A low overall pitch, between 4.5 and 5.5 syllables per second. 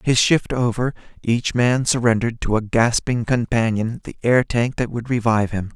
Yes: low, 115 Hz; 5.0 syllables/s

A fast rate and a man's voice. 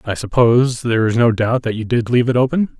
Yes: fast, 255 wpm; male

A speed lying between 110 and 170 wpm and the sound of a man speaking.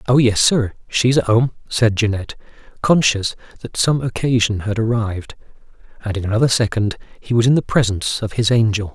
No: average, 180 wpm; male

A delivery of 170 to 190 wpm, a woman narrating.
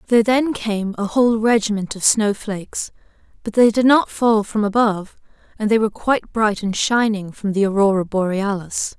Yes: average, 180 wpm; female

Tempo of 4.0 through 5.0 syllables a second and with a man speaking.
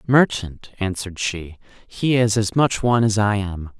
Yes: 4.5 syllables/s; male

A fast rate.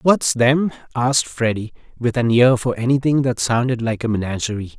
No: average, 175 wpm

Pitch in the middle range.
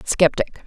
Yes: medium, 170 Hz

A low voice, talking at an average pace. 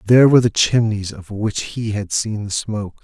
No: low, 105 Hz; fast, 220 wpm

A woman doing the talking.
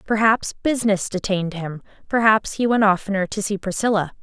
Yes: female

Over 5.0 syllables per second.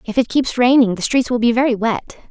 Yes: 5.6 syllables/s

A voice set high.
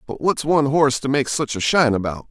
No: low, 135 Hz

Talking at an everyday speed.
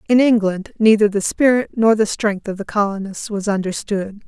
Yes: average, 180 wpm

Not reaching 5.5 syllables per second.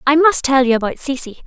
No: 6.0 syllables/s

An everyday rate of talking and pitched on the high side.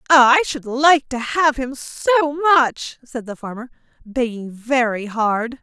Yes: average, 150 wpm; very high, 260 Hz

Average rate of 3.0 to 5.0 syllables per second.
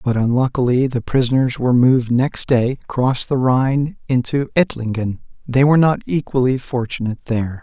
No: 5.4 syllables/s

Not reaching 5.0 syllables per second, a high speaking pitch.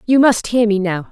No: 5.2 syllables/s; high, 215 Hz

